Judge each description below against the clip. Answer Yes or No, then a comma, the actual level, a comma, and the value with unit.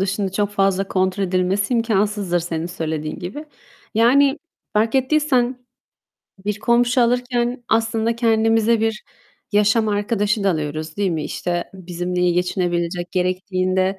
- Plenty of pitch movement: No, average, 4.1 semitones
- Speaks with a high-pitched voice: Yes, high, 200 Hz